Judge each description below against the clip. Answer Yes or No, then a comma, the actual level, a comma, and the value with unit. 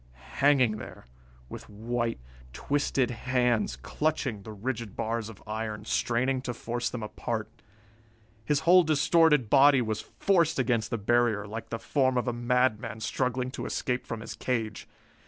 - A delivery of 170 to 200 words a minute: No, average, 150 wpm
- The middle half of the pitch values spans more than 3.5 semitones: No, average, 3.1 semitones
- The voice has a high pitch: No, low, 120 Hz